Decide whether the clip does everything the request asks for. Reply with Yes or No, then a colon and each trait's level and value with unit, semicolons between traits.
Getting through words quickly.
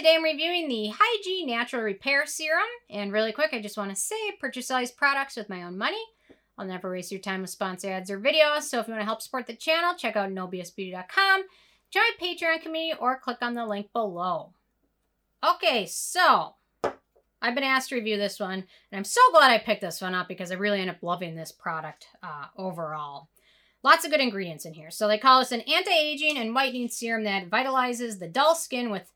Yes: fast, 215 wpm